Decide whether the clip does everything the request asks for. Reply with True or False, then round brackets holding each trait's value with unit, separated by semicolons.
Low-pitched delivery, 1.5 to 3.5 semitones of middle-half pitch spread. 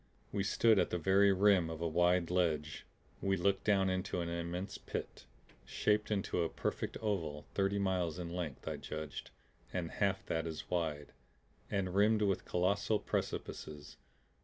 True (90 Hz; 2.9 semitones)